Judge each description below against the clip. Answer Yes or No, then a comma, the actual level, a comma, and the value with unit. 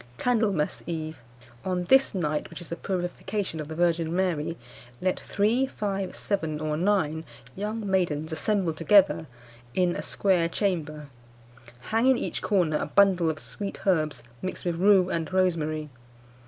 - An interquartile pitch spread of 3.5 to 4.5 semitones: Yes, average, 3.9 semitones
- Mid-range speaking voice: Yes, medium, 180 Hz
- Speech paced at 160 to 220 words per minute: No, average, 150 wpm